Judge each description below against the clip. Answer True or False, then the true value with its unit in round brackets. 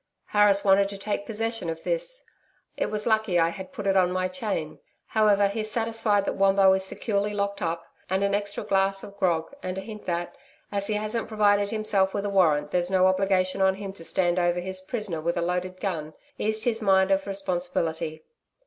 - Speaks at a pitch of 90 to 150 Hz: False (195 Hz)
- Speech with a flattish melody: True (2.2 semitones)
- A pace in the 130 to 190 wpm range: False (205 wpm)